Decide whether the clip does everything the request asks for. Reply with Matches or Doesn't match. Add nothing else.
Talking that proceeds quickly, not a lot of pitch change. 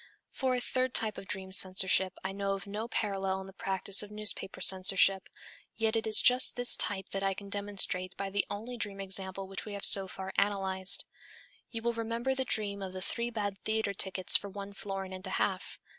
Matches